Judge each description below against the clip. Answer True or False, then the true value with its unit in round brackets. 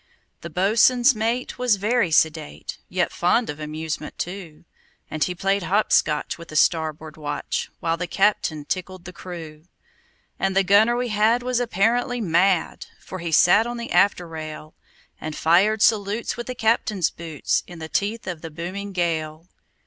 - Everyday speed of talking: True (165 wpm)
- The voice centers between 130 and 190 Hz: True (185 Hz)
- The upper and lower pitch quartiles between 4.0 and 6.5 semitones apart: True (5.2 semitones)